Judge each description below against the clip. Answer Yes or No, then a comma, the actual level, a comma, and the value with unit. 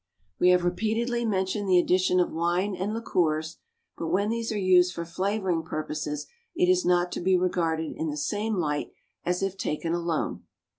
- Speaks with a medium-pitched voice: Yes, medium, 180 Hz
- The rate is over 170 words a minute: Yes, average, 180 wpm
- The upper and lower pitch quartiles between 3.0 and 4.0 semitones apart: Yes, average, 3.3 semitones